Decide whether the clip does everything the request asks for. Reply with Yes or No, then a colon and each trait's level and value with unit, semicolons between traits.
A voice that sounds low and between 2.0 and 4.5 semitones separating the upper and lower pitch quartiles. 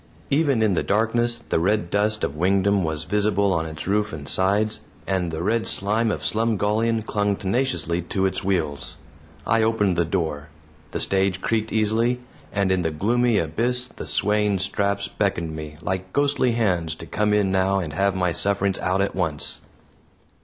Yes: low, 100 Hz; average, 3.4 semitones